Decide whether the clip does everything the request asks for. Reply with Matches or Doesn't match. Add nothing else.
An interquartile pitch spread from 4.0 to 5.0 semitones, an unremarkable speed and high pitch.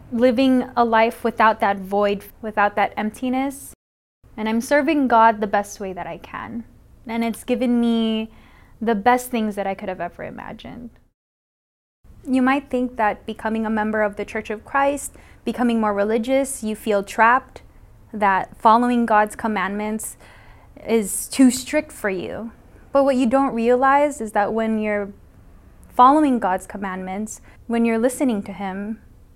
Doesn't match